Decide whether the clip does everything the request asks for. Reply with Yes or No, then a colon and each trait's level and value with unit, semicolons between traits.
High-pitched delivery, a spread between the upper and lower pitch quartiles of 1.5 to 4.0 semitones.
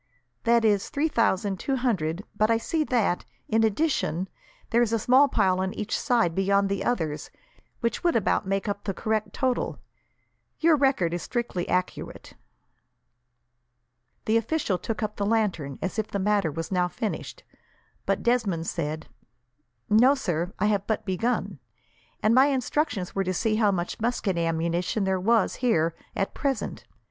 No: high, 210 Hz; average, 4.5 semitones